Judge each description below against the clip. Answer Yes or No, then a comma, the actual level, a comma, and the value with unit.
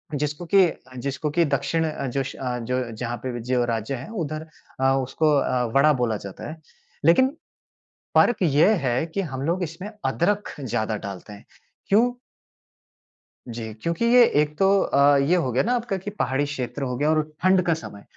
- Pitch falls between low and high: Yes, medium, 145 Hz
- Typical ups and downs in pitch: No, wide, 5.7 semitones